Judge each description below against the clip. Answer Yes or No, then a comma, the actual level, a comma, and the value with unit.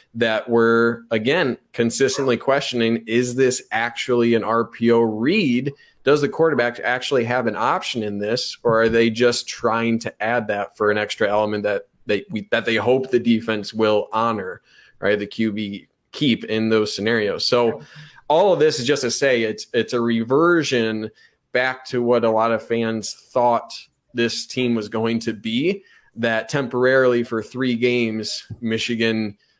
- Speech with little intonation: Yes, narrow, 1.9 semitones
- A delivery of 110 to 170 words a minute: Yes, average, 165 wpm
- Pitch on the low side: Yes, low, 115 Hz